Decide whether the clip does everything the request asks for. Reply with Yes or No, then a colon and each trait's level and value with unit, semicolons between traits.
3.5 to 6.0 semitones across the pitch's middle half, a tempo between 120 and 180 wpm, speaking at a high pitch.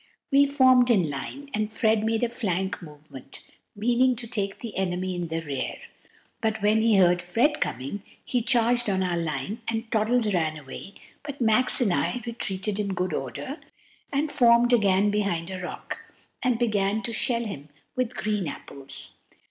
Yes: average, 5.0 semitones; average, 170 wpm; high, 210 Hz